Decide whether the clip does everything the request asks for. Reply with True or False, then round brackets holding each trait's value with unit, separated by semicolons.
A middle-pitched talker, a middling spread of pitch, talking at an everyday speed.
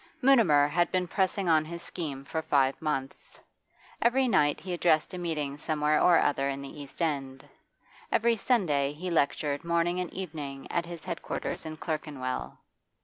True (160 Hz; 3.6 semitones; 165 wpm)